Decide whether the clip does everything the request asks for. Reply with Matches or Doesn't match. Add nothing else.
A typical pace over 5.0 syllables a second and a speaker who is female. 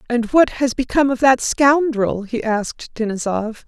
Doesn't match